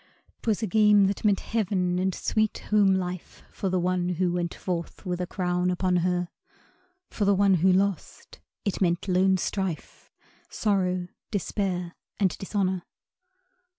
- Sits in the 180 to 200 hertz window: Yes, medium, 185 Hz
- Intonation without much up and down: Yes, narrow, 1.9 semitones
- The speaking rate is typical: Yes, average, 150 wpm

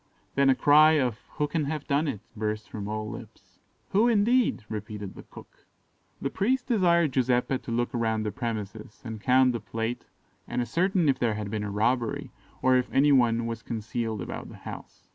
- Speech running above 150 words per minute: Yes, average, 190 wpm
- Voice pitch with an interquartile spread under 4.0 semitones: No, average, 5.1 semitones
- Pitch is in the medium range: No, low, 120 Hz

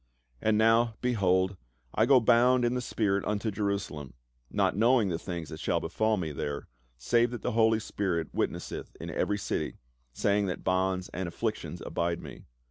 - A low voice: Yes, low, 100 Hz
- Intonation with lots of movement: No, average, 4.0 semitones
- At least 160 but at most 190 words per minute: Yes, average, 175 wpm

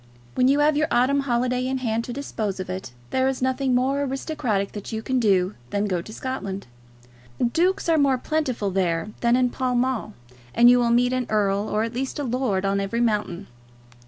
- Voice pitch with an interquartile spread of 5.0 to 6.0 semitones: No, average, 4.1 semitones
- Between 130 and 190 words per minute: No, fast, 205 wpm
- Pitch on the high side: Yes, high, 245 Hz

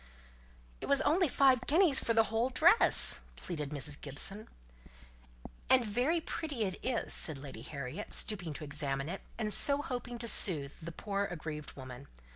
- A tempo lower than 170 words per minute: Yes, average, 160 wpm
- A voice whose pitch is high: Yes, high, 205 Hz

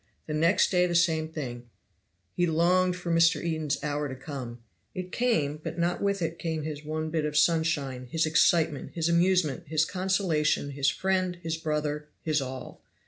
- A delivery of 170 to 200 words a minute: Yes, average, 175 wpm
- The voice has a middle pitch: Yes, medium, 160 Hz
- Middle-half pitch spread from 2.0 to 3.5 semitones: Yes, narrow, 2.6 semitones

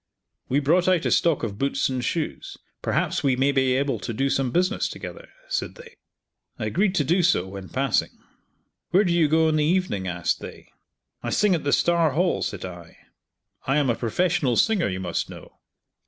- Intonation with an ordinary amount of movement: No, wide, 6.1 semitones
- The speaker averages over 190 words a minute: Yes, average, 200 wpm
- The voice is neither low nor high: Yes, medium, 145 Hz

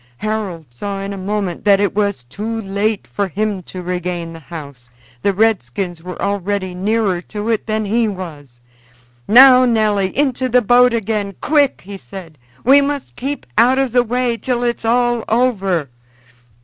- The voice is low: No, high, 205 Hz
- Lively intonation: No, average, 4.5 semitones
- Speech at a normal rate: Yes, average, 165 wpm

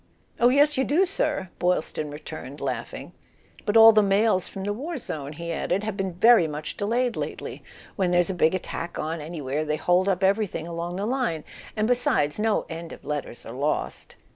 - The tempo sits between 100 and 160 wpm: No, average, 195 wpm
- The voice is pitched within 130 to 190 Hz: Yes, medium, 185 Hz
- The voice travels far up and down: Yes, wide, 6.0 semitones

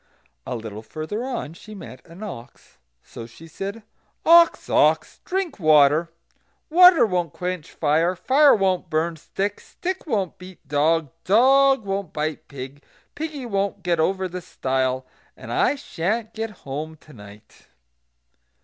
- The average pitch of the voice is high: No, medium, 180 Hz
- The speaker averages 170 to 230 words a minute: No, average, 140 wpm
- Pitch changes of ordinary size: No, wide, 6.4 semitones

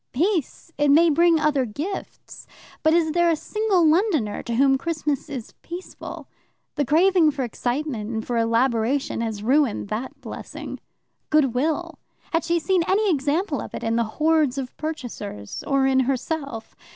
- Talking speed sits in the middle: Yes, average, 155 wpm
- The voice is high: Yes, very high, 290 Hz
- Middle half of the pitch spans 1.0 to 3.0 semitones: No, average, 5.2 semitones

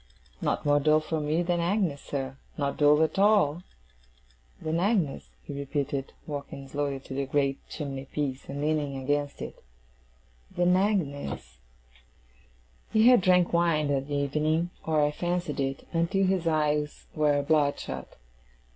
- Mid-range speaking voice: Yes, medium, 150 Hz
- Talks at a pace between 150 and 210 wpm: No, average, 140 wpm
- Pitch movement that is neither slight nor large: Yes, average, 3.2 semitones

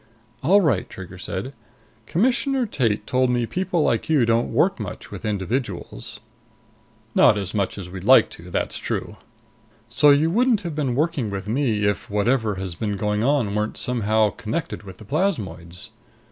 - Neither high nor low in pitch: No, low, 115 Hz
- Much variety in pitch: Yes, wide, 6.4 semitones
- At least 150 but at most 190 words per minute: Yes, average, 165 wpm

